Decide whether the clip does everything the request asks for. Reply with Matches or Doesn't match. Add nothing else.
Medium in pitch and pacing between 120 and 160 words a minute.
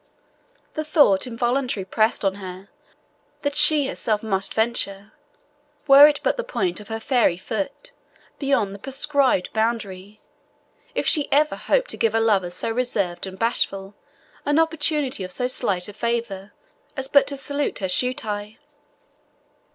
Doesn't match